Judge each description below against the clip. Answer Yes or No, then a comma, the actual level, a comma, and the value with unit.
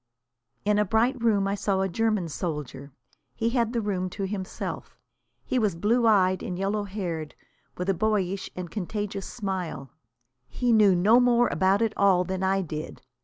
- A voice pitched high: Yes, high, 195 Hz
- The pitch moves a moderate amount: Yes, average, 3.0 semitones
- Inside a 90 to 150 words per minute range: No, average, 170 wpm